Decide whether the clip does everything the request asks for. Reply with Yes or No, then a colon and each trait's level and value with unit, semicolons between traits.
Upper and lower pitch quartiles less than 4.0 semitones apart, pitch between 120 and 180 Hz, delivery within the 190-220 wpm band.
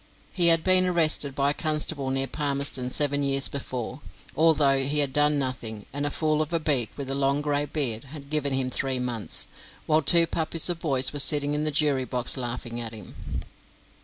Yes: narrow, 2.6 semitones; medium, 140 Hz; average, 200 wpm